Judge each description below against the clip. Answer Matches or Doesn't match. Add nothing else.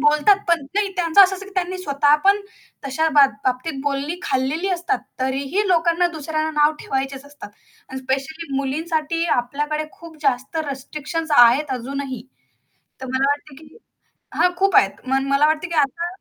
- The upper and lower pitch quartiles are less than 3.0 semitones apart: Doesn't match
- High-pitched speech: Matches